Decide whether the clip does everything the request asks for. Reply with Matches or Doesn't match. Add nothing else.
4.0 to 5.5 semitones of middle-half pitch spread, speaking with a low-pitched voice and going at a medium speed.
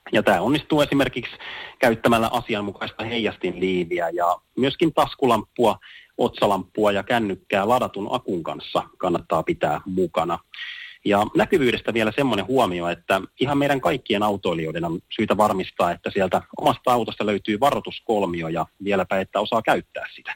Matches